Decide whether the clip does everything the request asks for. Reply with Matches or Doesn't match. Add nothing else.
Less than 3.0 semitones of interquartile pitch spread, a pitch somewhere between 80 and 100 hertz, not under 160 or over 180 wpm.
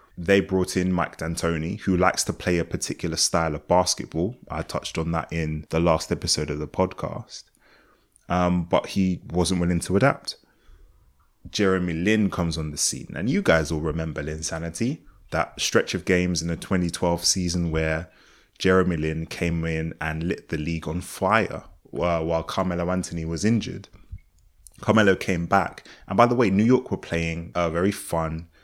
Matches